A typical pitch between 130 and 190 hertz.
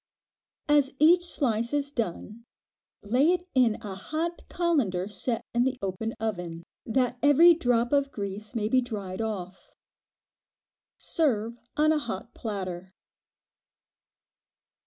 No: high, 235 Hz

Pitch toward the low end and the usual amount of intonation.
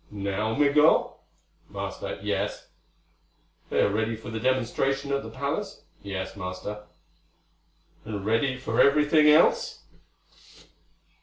Yes: low, 115 Hz; average, 5.0 semitones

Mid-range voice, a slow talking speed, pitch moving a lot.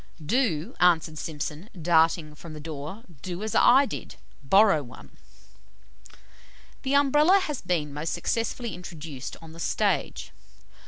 Yes: medium, 170 Hz; slow, 125 wpm; wide, 6.7 semitones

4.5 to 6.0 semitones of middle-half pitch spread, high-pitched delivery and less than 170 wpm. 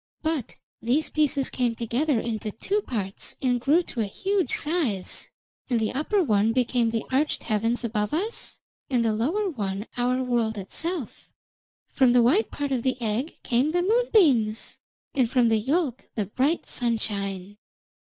Yes: wide, 5.4 semitones; high, 245 Hz; average, 160 wpm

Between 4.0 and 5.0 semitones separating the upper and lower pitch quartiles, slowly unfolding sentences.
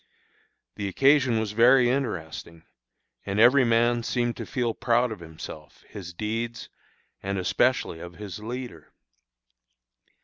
Yes: average, 4.3 semitones; slow, 125 wpm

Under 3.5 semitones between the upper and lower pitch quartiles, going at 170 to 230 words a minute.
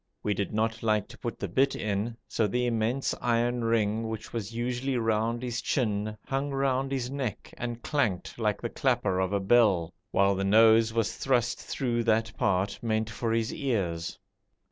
Yes: narrow, 2.4 semitones; average, 180 wpm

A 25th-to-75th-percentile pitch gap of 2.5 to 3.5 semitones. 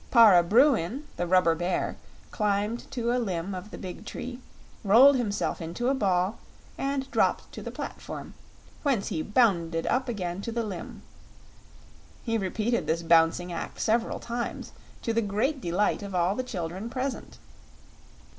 No: average, 5.2 semitones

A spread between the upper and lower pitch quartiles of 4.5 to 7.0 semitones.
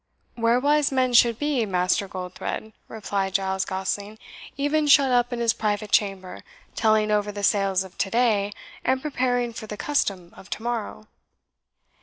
No: average, 3.9 semitones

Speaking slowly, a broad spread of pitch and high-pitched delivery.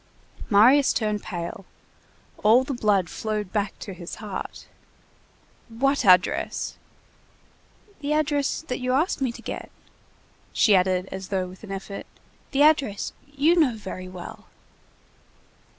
Yes: slow, 125 wpm; wide, 6.3 semitones; high, 215 Hz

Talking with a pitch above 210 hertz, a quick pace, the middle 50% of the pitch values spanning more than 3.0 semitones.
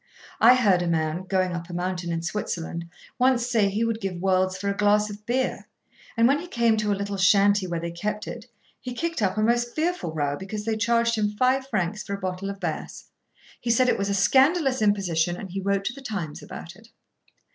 No: high, 205 Hz; fast, 225 wpm; average, 4.2 semitones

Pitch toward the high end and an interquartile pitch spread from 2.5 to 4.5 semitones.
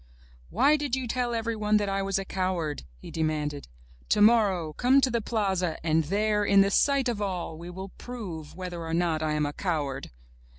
No: high, 195 Hz; average, 5.3 semitones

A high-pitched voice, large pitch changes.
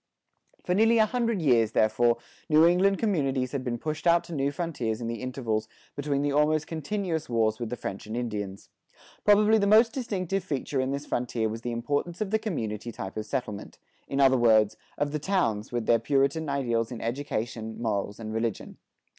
No: low, 135 Hz; wide, 6.7 semitones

